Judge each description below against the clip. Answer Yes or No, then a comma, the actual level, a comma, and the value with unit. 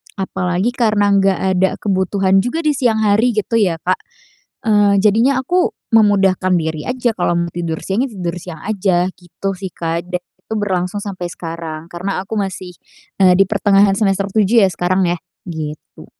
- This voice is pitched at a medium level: No, high, 195 Hz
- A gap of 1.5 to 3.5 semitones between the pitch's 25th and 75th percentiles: Yes, average, 2.9 semitones